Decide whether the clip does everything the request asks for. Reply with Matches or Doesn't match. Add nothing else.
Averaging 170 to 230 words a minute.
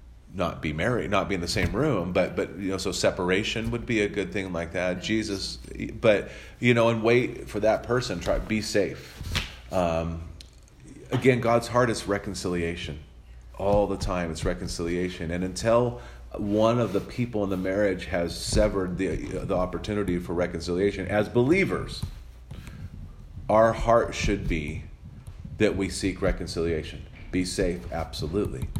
Doesn't match